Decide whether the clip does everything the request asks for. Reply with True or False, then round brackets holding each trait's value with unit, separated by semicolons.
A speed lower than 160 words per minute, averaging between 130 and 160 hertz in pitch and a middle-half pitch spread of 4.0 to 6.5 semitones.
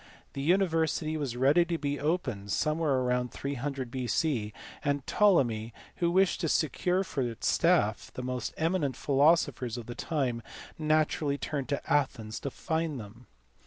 True (150 wpm; 140 Hz; 4.3 semitones)